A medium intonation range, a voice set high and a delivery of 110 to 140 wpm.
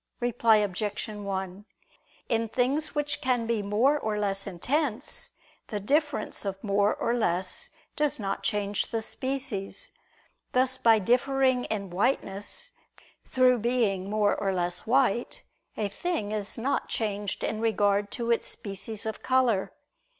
Yes: average, 4.0 semitones; high, 220 Hz; slow, 135 wpm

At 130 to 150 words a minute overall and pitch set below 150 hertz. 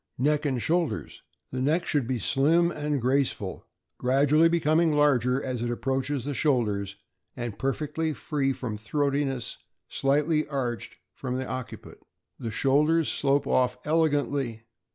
Yes: slow, 135 wpm; medium, 140 Hz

